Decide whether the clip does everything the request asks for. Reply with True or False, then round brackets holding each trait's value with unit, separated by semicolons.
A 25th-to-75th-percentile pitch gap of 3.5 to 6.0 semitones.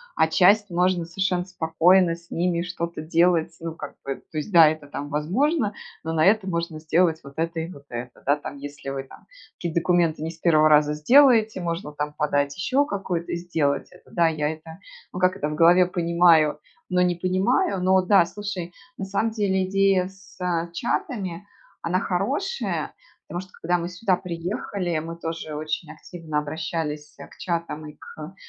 False (3.0 semitones)